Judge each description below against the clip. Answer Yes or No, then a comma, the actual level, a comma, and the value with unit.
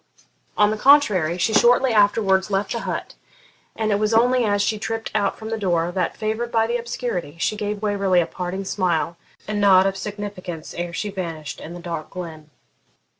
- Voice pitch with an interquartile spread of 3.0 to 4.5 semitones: Yes, average, 3.5 semitones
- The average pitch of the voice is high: Yes, high, 200 Hz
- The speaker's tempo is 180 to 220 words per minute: Yes, average, 190 wpm